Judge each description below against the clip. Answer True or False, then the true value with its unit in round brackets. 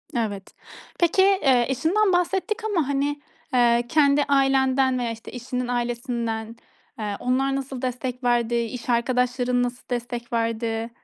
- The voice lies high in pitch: True (250 Hz)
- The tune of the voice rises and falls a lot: False (2.5 semitones)